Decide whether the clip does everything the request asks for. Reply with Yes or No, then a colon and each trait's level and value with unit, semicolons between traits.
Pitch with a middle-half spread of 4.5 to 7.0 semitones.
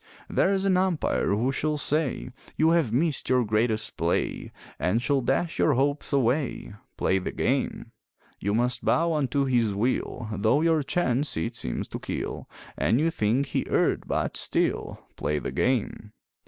Yes: average, 5.3 semitones